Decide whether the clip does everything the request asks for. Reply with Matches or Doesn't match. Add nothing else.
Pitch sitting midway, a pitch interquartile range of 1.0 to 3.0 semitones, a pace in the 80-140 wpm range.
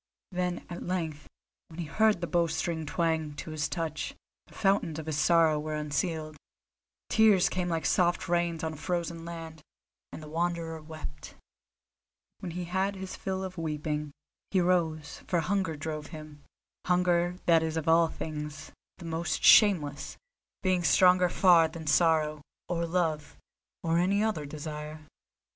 Doesn't match